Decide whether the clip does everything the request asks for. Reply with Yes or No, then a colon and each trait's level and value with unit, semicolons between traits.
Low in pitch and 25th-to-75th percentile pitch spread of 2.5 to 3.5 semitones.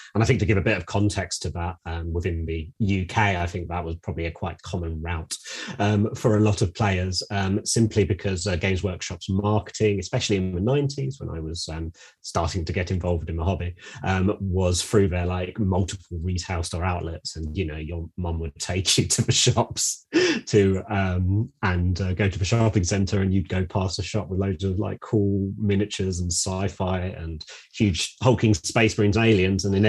Yes: very low, 95 Hz; average, 2.9 semitones